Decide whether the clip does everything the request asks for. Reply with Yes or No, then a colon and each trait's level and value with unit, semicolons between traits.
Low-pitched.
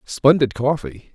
Yes: low, 125 Hz